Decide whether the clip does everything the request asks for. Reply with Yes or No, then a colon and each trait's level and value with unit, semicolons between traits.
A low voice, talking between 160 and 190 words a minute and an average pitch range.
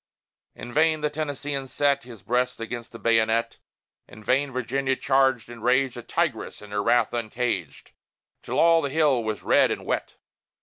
Yes: low, 125 Hz; average, 170 wpm; average, 3.3 semitones